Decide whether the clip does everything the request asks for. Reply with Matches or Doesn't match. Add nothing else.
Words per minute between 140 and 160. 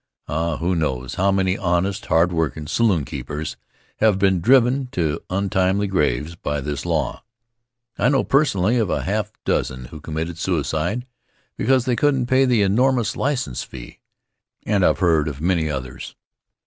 Matches